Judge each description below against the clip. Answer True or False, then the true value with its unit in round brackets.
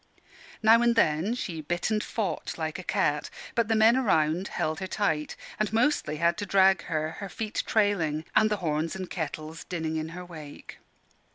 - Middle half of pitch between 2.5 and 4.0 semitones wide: False (5.2 semitones)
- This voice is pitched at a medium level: True (180 Hz)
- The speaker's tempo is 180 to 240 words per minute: True (185 wpm)